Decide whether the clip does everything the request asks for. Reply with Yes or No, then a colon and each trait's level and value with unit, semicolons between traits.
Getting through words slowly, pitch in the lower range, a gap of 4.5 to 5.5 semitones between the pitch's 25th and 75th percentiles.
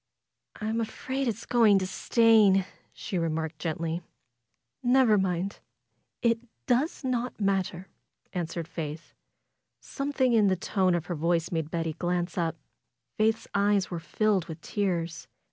No: slow, 130 wpm; high, 190 Hz; average, 4.9 semitones